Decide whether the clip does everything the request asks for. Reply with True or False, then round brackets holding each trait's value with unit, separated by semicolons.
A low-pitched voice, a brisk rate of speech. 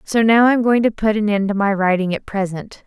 False (210 Hz; 295 wpm)